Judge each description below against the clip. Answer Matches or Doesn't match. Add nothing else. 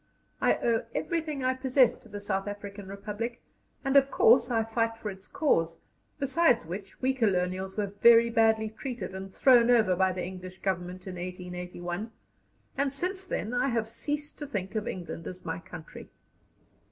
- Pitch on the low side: Doesn't match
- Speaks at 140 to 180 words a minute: Matches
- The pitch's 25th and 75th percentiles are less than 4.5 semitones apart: Doesn't match